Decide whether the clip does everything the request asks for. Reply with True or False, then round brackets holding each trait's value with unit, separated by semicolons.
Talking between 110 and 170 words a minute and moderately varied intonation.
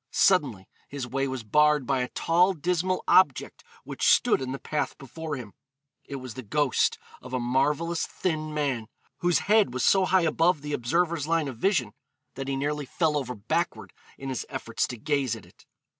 False (190 wpm; 4.3 semitones)